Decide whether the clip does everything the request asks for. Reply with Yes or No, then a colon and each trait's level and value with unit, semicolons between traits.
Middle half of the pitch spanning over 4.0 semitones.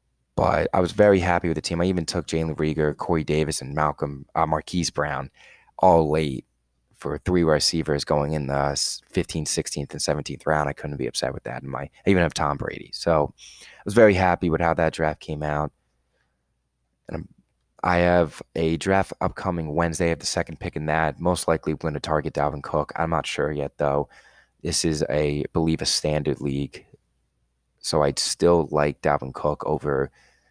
No: average, 2.9 semitones